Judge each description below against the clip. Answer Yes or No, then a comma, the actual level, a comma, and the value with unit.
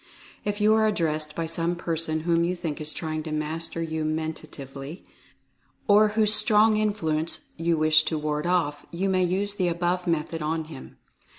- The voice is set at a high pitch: No, medium, 165 Hz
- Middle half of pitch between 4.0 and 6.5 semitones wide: No, average, 2.9 semitones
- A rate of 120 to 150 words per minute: No, average, 175 wpm